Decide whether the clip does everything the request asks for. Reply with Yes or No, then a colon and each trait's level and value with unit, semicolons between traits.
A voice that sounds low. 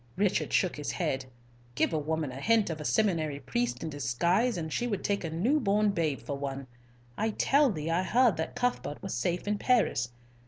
No: medium, 165 Hz